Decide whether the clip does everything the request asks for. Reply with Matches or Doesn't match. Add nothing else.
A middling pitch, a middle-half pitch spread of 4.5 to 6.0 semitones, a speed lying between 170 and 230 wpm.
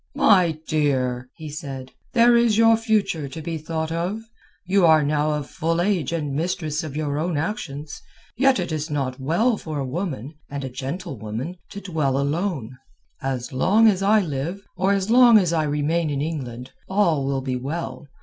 Matches